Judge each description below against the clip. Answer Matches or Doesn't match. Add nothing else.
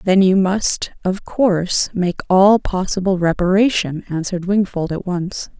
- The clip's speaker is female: Matches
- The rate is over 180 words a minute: Doesn't match